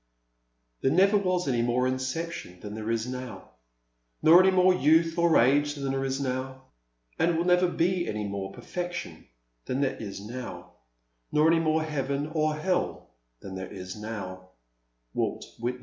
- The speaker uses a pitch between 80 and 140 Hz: Yes, low, 135 Hz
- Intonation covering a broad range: Yes, wide, 7.4 semitones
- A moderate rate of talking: Yes, average, 165 wpm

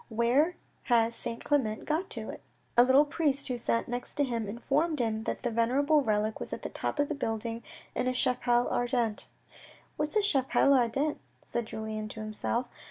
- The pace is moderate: Yes, average, 190 wpm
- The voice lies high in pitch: Yes, high, 245 Hz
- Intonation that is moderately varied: Yes, average, 3.8 semitones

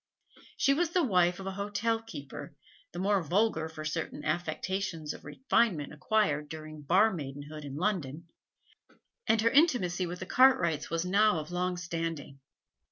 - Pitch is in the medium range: Yes, medium, 175 Hz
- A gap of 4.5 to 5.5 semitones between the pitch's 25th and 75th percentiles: Yes, average, 5.1 semitones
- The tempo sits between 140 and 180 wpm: Yes, average, 155 wpm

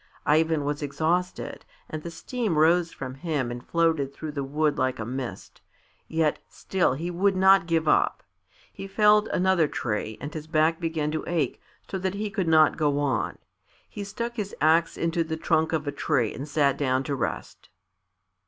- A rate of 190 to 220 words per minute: No, average, 180 wpm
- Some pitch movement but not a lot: Yes, average, 3.5 semitones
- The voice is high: No, medium, 160 Hz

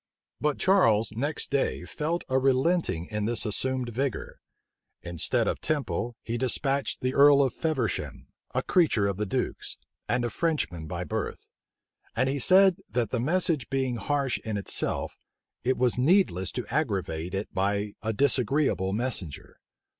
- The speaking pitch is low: Yes, low, 125 Hz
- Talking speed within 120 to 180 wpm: Yes, average, 150 wpm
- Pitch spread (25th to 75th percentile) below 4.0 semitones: No, average, 5.2 semitones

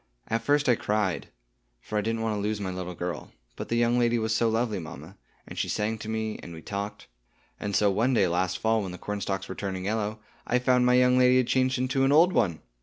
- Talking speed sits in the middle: No, fast, 245 wpm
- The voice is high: No, low, 110 Hz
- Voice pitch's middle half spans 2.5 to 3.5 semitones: No, average, 4.0 semitones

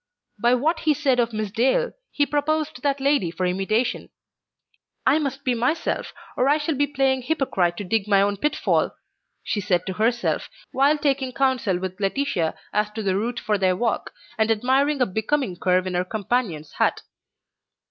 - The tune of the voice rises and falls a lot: Yes, wide, 6.2 semitones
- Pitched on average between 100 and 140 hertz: No, high, 240 Hz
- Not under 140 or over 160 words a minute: No, average, 180 wpm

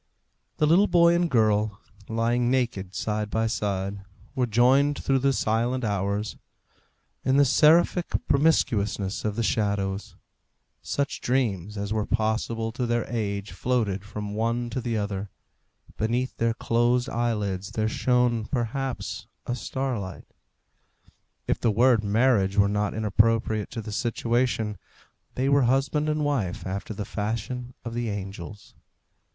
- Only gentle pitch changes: No, average, 3.4 semitones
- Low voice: Yes, low, 115 Hz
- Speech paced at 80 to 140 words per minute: Yes, slow, 135 wpm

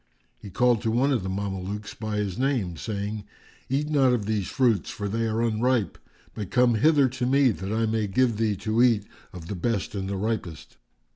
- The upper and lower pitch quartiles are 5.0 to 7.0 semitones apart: No, average, 3.5 semitones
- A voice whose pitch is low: Yes, low, 110 Hz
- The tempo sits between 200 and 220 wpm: Yes, fast, 205 wpm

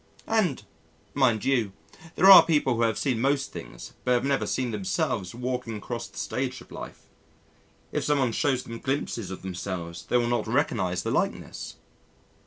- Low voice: Yes, low, 120 Hz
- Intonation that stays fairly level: No, average, 3.9 semitones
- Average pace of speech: Yes, average, 170 wpm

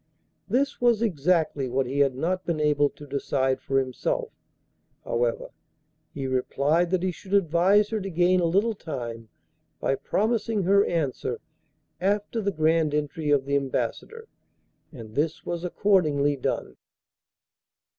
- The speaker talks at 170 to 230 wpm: No, average, 140 wpm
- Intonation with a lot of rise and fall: Yes, wide, 5.7 semitones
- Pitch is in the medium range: Yes, medium, 160 Hz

